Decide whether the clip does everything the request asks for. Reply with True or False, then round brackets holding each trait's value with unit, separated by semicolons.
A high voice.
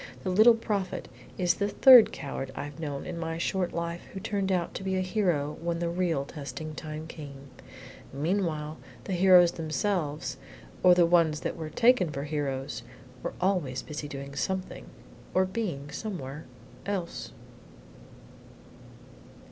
False (170 Hz)